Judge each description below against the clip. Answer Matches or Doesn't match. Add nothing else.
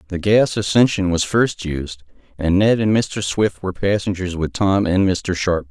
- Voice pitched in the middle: Doesn't match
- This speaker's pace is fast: Doesn't match